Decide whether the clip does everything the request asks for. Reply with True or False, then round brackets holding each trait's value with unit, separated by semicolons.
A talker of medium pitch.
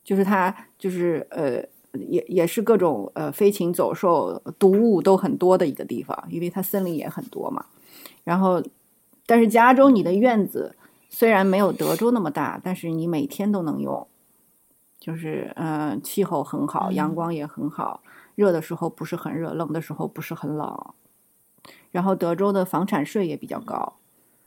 True (180 Hz)